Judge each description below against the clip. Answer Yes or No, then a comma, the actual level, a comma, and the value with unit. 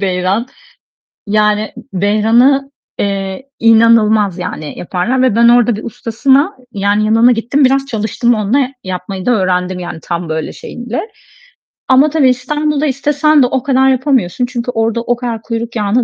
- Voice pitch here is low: No, high, 230 Hz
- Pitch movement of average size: Yes, average, 4.3 semitones